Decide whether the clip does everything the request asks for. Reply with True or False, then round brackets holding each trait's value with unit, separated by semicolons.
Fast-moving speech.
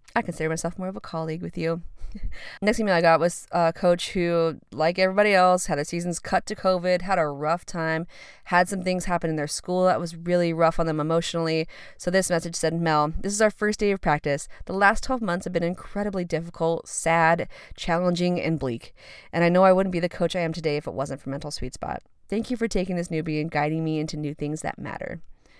True (235 wpm)